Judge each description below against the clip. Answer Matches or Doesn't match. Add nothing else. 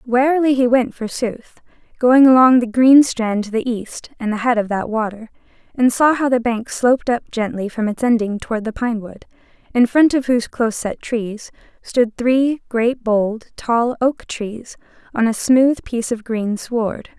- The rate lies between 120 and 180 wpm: Doesn't match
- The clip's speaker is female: Matches